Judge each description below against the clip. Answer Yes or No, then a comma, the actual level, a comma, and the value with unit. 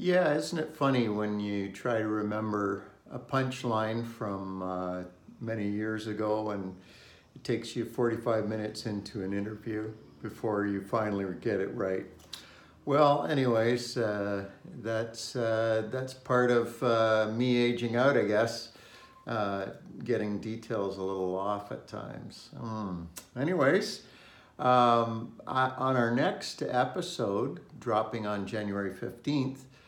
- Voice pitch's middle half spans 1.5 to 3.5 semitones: Yes, average, 3.0 semitones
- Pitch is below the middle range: Yes, low, 110 Hz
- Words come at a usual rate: No, slow, 130 wpm